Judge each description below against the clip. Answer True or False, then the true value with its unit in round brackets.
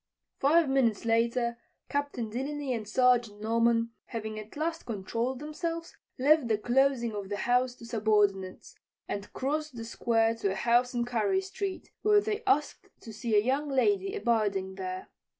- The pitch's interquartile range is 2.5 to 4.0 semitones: False (4.7 semitones)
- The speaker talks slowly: False (160 wpm)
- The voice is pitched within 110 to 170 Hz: False (240 Hz)